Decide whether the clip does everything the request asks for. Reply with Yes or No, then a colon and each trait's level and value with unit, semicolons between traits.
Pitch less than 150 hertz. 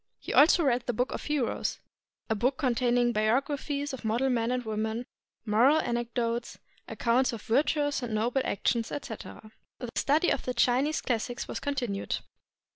No: high, 245 Hz